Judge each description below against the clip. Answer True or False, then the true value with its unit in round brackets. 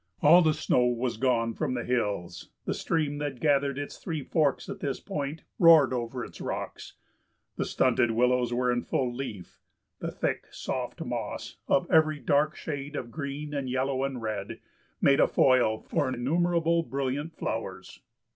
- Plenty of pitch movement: False (3.4 semitones)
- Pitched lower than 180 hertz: True (135 Hz)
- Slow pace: False (165 wpm)